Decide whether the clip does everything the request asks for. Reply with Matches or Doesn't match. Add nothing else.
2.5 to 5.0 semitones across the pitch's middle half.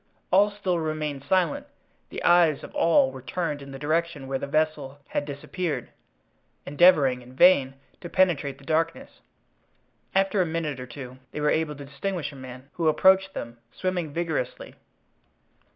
Matches